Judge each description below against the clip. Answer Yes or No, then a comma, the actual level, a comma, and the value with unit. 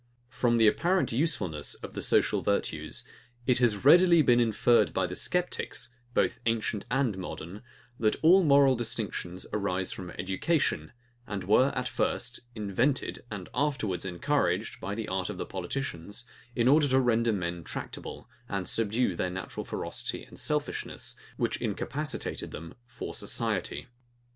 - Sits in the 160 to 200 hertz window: No, low, 115 Hz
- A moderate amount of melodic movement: No, wide, 5.7 semitones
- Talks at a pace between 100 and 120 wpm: No, average, 140 wpm